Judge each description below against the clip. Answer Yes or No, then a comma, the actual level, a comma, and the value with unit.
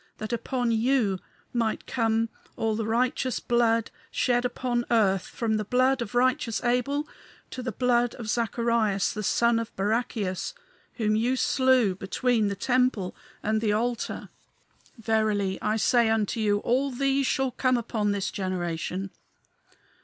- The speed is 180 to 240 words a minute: No, average, 145 wpm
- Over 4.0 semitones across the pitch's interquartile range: No, average, 2.8 semitones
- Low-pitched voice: No, high, 230 Hz